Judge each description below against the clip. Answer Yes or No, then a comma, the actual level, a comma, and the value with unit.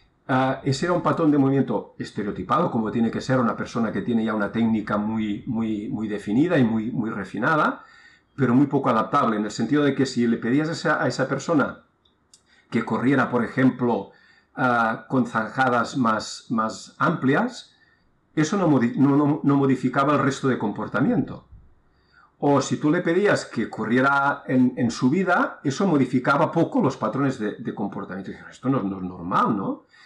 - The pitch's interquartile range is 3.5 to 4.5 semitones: Yes, average, 3.9 semitones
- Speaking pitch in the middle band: No, low, 130 Hz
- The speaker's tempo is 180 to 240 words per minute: Yes, average, 185 wpm